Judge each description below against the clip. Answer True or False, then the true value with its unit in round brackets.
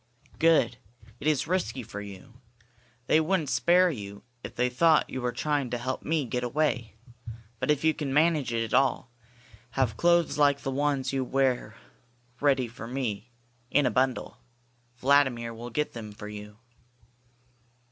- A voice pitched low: True (130 Hz)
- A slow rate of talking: False (160 wpm)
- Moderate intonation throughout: True (4.1 semitones)